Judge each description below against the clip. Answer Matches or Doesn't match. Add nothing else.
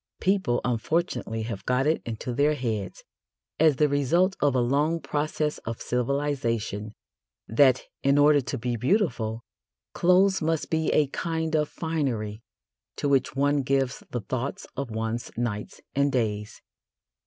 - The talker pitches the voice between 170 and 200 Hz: Doesn't match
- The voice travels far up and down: Doesn't match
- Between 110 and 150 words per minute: Matches